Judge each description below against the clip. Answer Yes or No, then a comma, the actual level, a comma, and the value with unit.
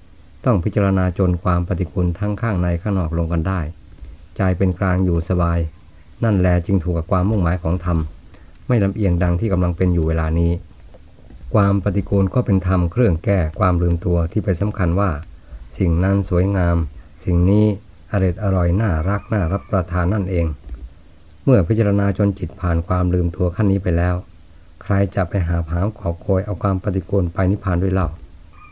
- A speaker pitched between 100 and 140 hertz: No, very low, 90 Hz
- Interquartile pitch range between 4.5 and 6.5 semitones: No, average, 2.7 semitones